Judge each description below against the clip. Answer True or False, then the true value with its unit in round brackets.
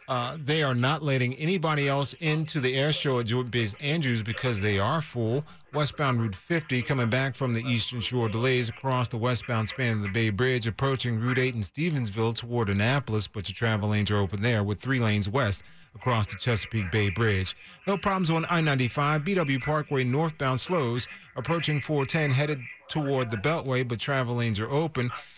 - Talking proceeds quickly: False (190 wpm)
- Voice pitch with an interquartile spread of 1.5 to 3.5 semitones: False (4.3 semitones)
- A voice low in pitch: True (125 Hz)